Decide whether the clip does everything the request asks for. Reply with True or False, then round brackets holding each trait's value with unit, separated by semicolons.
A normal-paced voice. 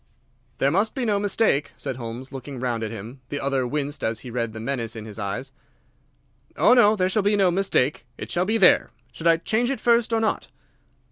False (215 wpm)